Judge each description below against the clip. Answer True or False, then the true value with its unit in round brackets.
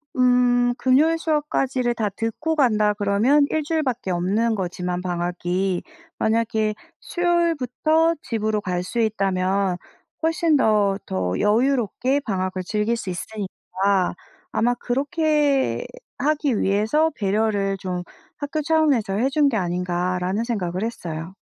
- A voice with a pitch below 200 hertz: False (220 Hz)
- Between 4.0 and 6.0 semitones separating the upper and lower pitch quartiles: False (6.5 semitones)